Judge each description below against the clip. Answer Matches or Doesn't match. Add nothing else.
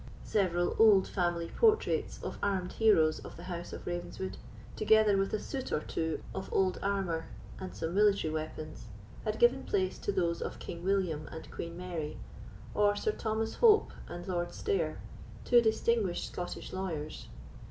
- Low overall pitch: Doesn't match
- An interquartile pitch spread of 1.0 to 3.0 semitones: Doesn't match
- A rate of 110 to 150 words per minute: Doesn't match